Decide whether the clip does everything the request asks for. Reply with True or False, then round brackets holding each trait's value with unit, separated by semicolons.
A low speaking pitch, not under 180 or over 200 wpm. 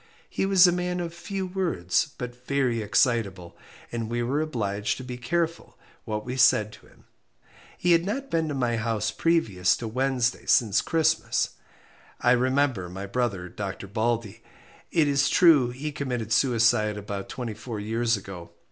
False (120 Hz; 165 wpm)